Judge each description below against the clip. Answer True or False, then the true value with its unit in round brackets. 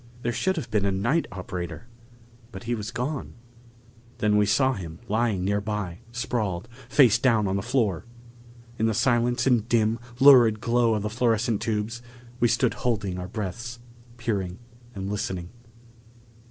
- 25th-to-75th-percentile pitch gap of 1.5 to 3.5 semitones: True (3.2 semitones)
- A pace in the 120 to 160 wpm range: True (155 wpm)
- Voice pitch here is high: False (110 Hz)